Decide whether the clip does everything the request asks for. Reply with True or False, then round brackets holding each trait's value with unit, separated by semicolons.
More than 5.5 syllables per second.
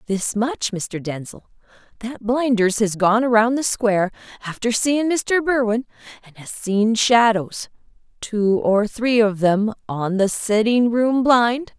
False (3.7 syllables/s)